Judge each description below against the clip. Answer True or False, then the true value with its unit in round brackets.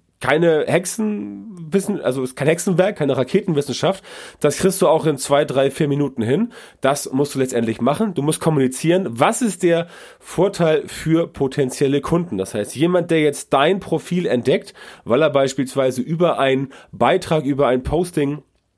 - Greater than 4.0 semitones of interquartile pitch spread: True (4.5 semitones)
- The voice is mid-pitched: True (150 Hz)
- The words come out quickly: False (165 wpm)